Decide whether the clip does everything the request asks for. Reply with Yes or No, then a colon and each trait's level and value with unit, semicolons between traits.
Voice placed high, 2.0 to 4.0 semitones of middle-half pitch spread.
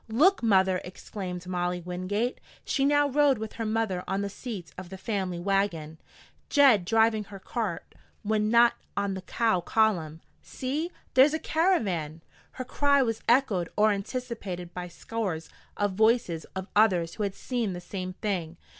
No: high, 205 Hz; average, 4.5 semitones